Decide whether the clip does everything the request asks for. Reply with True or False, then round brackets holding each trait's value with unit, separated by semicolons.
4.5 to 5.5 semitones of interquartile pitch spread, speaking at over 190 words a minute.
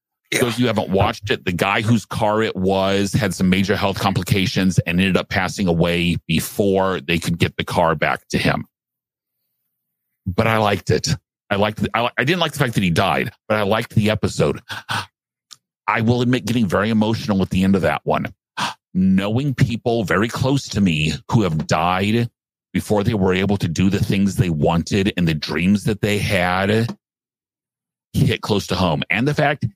False (3.6 semitones; 200 wpm)